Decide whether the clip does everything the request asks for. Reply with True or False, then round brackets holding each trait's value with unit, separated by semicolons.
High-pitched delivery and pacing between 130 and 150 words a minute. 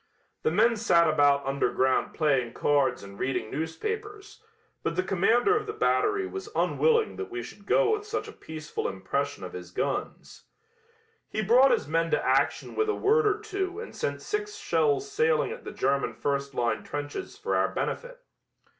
False (225 Hz; 175 wpm)